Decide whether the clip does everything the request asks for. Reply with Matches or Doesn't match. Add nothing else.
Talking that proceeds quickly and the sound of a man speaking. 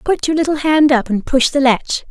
Doesn't match